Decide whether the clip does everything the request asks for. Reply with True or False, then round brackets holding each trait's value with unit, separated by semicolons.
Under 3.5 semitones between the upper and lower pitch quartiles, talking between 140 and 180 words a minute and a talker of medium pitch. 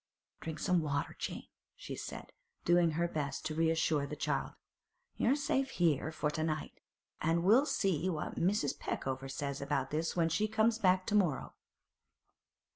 False (3.9 semitones; 155 wpm; 165 Hz)